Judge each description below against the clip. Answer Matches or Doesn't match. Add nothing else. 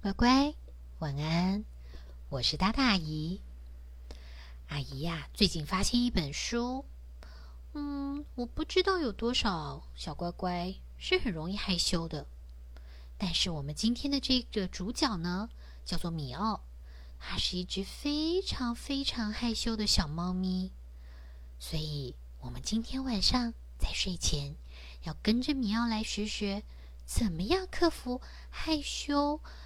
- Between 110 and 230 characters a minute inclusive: Matches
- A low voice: Doesn't match